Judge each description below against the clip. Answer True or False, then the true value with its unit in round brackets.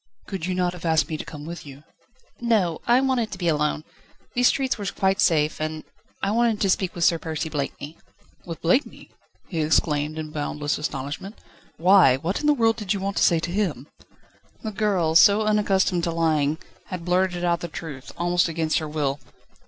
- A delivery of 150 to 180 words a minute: False (190 wpm)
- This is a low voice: False (170 Hz)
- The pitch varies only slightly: False (4.1 semitones)